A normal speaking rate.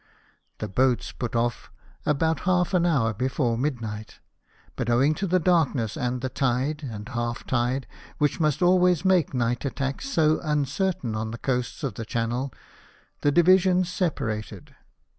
Yes: average, 155 wpm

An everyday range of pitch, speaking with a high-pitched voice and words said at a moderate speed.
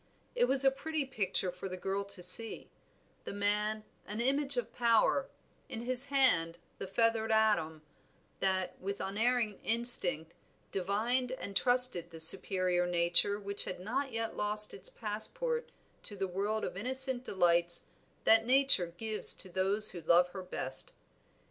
Yes: average, 4.9 semitones; high, 210 Hz; average, 150 wpm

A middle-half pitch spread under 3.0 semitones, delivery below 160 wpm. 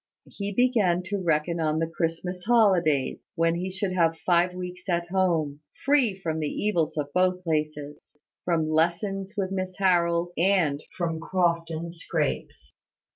Yes: narrow, 2.5 semitones; average, 145 wpm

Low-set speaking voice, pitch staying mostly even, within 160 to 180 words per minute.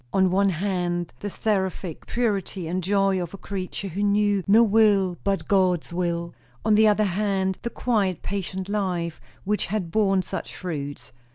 No: high, 195 Hz; narrow, 2.3 semitones; average, 165 wpm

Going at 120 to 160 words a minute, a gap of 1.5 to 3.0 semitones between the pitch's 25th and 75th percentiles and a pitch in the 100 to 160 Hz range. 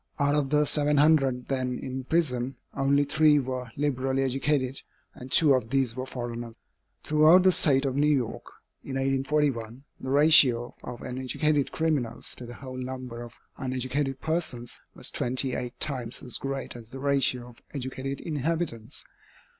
Yes: average, 155 wpm; narrow, 2.5 semitones; low, 135 Hz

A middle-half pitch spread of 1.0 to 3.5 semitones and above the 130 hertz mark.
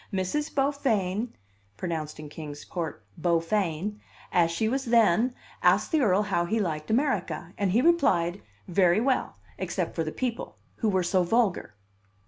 No: average, 5.3 semitones; high, 190 Hz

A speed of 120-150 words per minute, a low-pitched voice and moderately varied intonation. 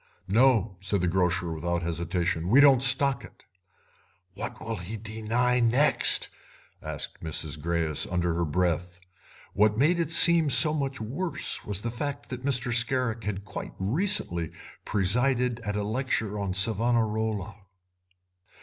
No: average, 140 wpm; low, 110 Hz; wide, 5.7 semitones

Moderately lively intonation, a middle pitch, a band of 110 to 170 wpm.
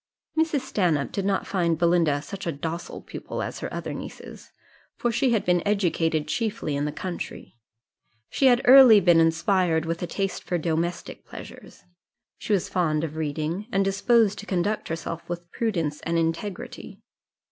Yes: average, 4.1 semitones; medium, 175 Hz; average, 165 wpm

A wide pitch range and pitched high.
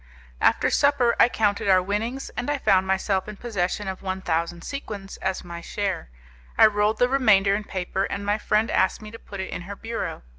No: average, 2.8 semitones; high, 200 Hz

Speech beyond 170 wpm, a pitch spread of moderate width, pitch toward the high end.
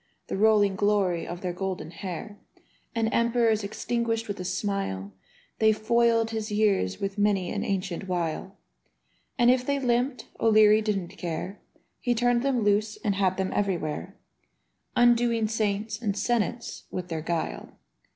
No: average, 145 wpm; average, 3.3 semitones; high, 210 Hz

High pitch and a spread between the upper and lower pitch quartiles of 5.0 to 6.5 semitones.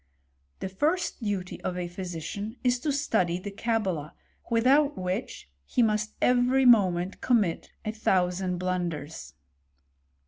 Yes: high, 200 Hz; average, 5.3 semitones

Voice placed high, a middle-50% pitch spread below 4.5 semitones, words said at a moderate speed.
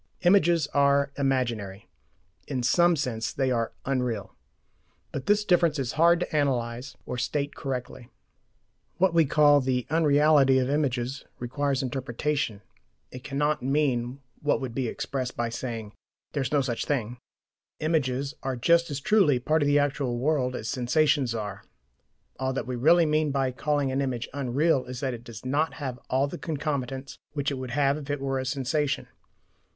No: low, 135 Hz; average, 2.8 semitones; average, 165 wpm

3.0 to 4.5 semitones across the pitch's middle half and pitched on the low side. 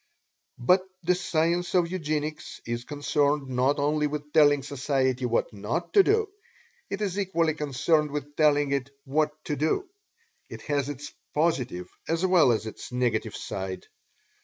No: average, 3.6 semitones; medium, 145 Hz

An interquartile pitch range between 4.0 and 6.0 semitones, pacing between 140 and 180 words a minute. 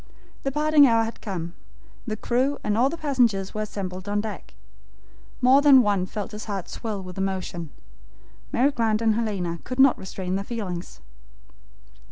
Yes: average, 4.6 semitones; average, 170 wpm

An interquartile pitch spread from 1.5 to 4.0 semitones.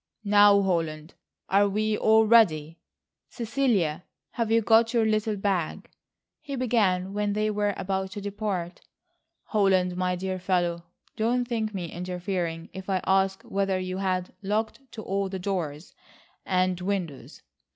Yes: average, 2.8 semitones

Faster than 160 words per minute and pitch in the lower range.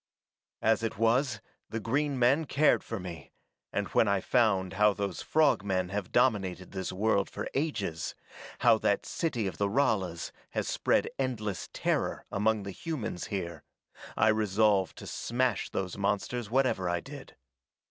No: average, 155 wpm; low, 105 Hz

